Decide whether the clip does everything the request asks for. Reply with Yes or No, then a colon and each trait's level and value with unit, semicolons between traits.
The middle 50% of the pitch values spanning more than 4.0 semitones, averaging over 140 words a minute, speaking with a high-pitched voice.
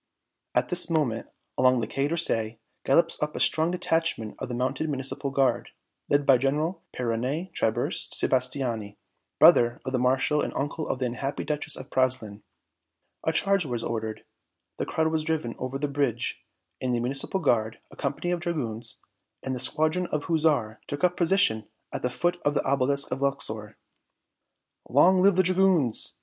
No: average, 4.6 semitones; average, 170 wpm; low, 135 Hz